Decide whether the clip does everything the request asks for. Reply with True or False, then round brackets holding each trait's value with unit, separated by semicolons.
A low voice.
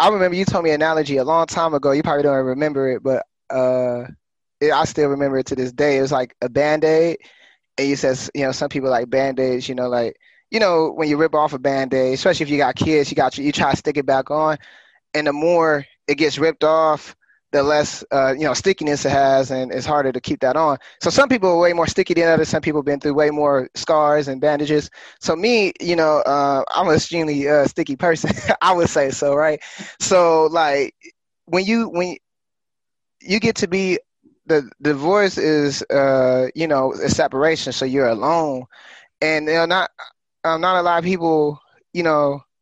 False (150 Hz)